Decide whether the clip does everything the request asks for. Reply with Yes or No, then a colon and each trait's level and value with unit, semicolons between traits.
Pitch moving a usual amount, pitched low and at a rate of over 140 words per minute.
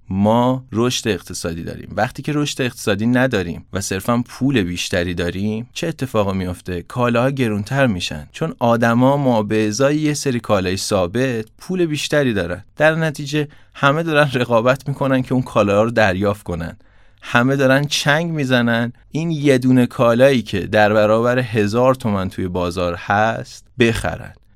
Yes: average, 4.7 semitones; low, 120 Hz; average, 150 wpm